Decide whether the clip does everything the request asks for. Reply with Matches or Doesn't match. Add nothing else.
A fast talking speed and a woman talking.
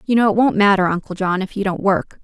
Matches